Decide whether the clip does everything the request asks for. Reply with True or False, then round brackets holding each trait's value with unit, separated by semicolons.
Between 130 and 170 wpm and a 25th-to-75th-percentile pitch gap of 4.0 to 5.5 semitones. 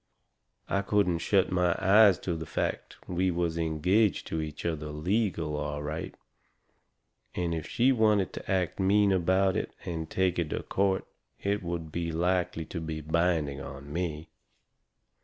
False (155 wpm; 3.1 semitones)